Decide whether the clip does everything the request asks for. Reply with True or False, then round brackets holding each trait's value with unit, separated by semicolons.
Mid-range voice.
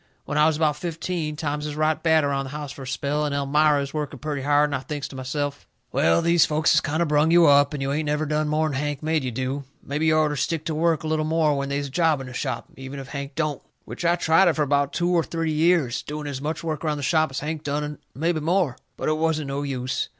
True (150 Hz)